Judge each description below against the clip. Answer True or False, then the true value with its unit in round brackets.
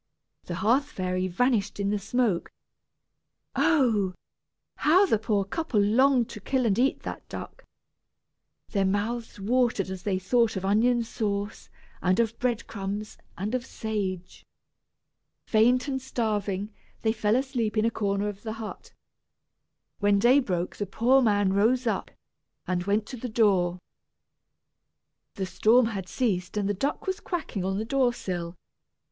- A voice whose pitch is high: True (215 Hz)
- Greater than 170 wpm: False (150 wpm)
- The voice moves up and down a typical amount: True (3.7 semitones)